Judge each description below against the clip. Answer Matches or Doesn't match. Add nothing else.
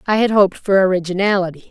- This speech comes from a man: Doesn't match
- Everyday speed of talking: Matches